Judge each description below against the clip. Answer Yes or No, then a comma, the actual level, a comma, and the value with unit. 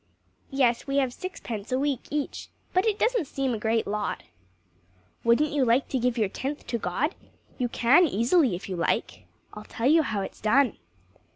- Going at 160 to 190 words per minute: Yes, average, 185 wpm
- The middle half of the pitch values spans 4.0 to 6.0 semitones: Yes, average, 4.4 semitones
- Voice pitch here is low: No, very high, 255 Hz